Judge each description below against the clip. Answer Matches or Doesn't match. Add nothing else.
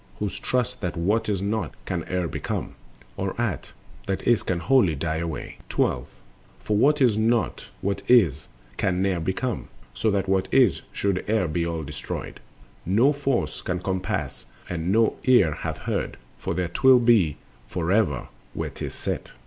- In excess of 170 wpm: Doesn't match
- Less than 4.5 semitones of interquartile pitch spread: Doesn't match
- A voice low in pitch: Matches